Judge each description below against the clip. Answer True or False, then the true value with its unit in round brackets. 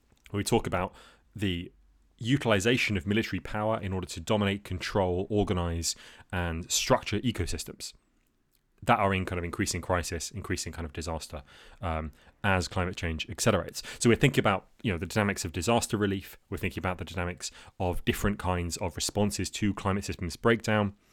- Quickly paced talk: False (170 wpm)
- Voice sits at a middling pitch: False (95 Hz)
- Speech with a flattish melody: False (3.4 semitones)